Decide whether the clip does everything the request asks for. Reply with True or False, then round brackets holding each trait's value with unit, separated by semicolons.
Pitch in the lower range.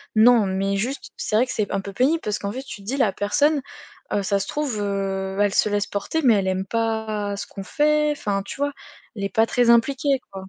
False (215 Hz)